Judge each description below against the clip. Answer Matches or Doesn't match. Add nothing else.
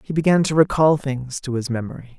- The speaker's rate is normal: Doesn't match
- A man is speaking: Matches